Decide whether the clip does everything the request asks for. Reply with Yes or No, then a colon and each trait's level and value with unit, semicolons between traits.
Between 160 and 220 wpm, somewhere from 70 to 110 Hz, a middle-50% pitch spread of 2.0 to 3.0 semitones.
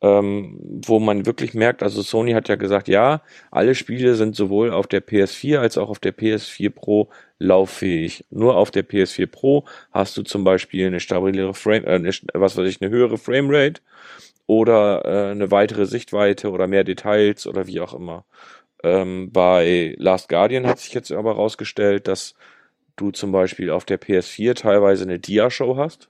Yes: average, 175 wpm; low, 100 Hz; average, 2.7 semitones